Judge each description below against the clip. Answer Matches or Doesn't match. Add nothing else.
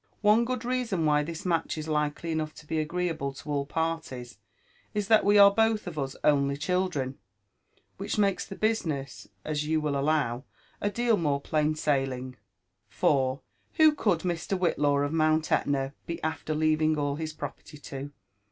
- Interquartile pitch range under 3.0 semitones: Doesn't match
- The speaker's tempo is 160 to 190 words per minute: Matches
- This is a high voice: Doesn't match